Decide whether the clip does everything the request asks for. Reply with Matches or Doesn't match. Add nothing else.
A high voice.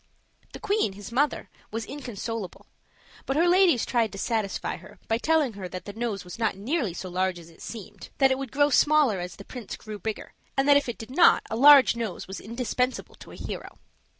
Matches